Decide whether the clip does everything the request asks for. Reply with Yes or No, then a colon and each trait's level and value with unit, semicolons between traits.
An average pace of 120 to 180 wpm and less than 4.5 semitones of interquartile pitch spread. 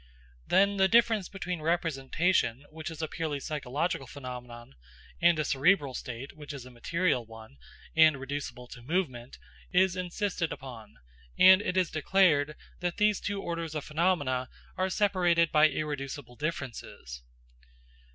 No: average, 140 wpm; average, 5.3 semitones